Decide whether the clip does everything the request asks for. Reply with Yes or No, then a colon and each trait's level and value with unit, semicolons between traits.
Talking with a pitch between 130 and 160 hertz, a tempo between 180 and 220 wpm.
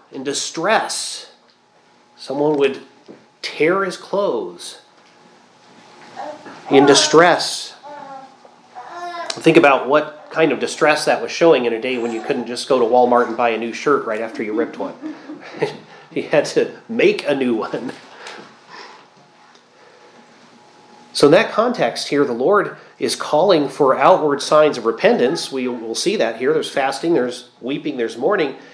No: medium, 140 Hz; average, 145 wpm